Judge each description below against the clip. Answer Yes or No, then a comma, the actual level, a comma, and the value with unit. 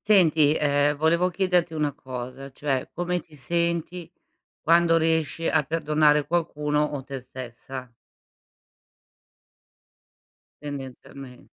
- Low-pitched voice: No, medium, 150 Hz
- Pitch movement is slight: No, average, 3.5 semitones